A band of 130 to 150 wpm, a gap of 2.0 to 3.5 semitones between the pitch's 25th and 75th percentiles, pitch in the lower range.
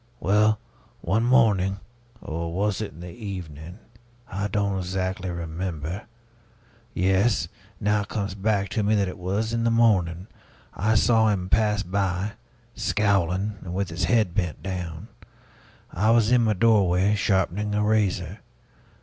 Yes: average, 145 wpm; average, 2.9 semitones; low, 100 Hz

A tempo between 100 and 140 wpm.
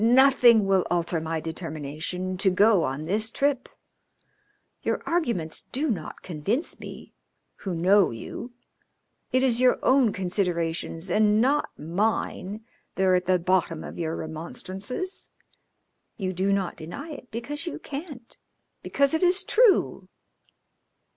Yes: slow, 135 wpm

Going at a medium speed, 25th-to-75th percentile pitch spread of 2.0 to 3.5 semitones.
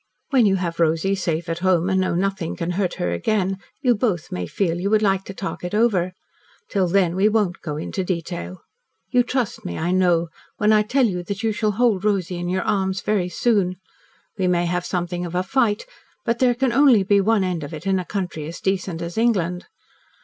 No: fast, 220 wpm; average, 3.1 semitones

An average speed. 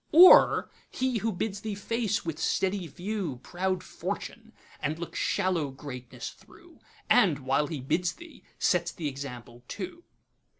No: slow, 130 wpm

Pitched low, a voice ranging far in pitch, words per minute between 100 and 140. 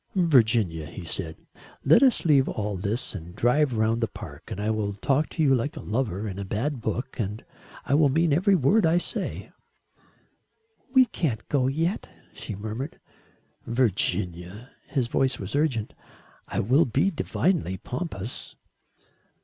No: low, 125 Hz; wide, 6.3 semitones; average, 155 wpm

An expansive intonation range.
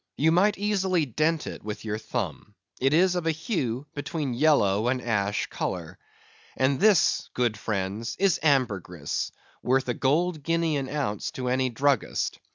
Yes: wide, 6.3 semitones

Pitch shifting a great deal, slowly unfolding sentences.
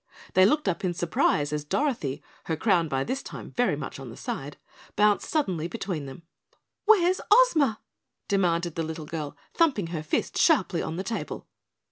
No: wide, 7.4 semitones; average, 170 wpm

